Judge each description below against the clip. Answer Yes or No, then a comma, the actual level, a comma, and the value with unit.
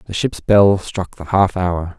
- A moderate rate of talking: No, fast, 210 wpm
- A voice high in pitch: No, very low, 95 Hz